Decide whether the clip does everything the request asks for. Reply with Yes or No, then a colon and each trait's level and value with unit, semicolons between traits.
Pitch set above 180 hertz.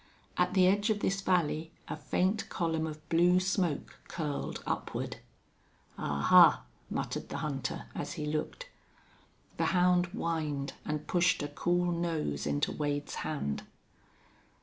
No: medium, 165 Hz